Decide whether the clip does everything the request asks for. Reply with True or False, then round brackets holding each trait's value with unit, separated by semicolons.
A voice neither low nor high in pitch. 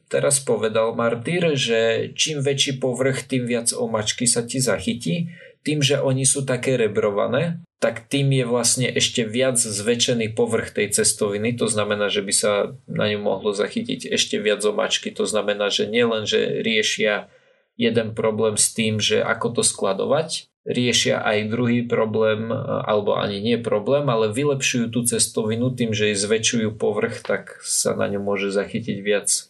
False (120 Hz)